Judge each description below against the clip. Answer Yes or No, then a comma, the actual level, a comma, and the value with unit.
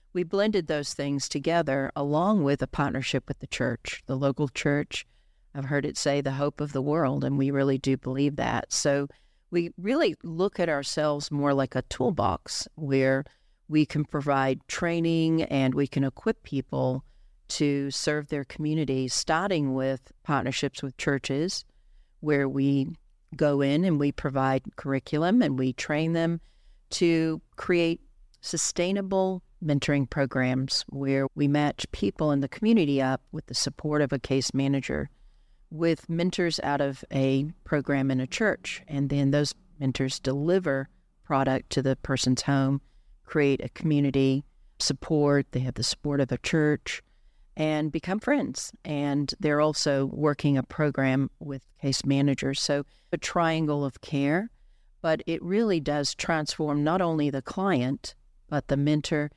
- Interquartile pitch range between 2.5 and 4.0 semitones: Yes, average, 2.8 semitones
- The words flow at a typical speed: Yes, average, 150 wpm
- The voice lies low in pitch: No, medium, 145 Hz